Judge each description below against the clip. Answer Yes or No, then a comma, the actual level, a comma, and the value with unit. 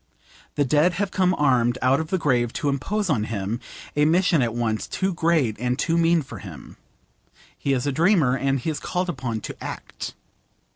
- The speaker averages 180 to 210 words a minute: Yes, average, 195 wpm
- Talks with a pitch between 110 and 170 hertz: Yes, medium, 140 Hz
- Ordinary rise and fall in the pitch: No, wide, 5.7 semitones